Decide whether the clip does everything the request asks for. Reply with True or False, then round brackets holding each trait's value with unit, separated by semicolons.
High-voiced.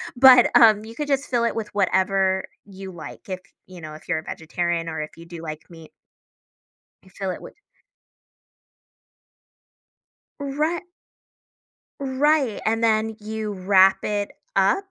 True (200 Hz)